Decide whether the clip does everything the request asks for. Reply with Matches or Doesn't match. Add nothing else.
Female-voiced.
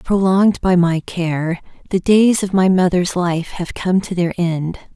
Matches